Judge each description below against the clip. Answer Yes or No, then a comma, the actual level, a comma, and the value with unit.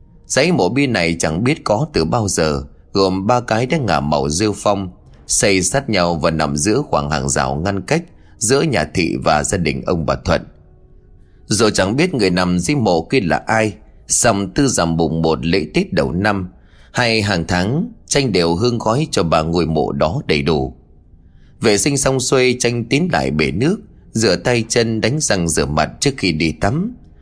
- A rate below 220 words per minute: Yes, average, 200 wpm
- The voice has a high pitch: No, very low, 95 Hz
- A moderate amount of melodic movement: No, wide, 7.3 semitones